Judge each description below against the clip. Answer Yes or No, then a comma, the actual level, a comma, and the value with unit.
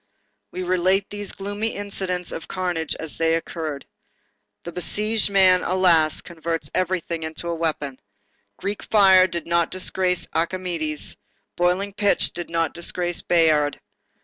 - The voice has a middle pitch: Yes, medium, 175 Hz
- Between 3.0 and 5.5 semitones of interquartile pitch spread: No, narrow, 2.4 semitones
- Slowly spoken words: Yes, slow, 130 wpm